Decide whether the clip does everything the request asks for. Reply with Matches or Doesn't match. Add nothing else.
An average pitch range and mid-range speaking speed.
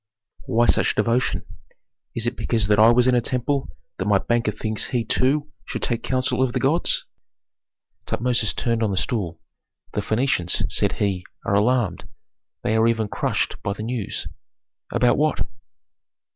Matches